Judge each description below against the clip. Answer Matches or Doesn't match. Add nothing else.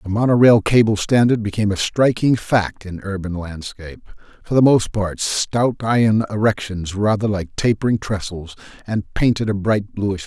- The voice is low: Matches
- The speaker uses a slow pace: Doesn't match